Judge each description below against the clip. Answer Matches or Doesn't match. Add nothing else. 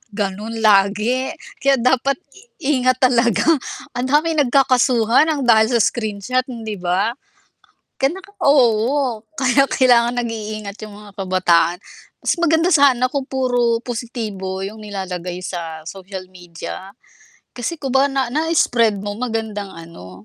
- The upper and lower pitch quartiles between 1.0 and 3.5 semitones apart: Doesn't match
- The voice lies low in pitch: Doesn't match